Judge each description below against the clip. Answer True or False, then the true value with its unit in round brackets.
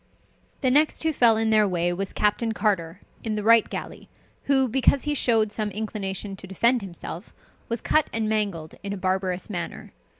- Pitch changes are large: False (3.3 semitones)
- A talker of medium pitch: False (215 Hz)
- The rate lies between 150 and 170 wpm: False (180 wpm)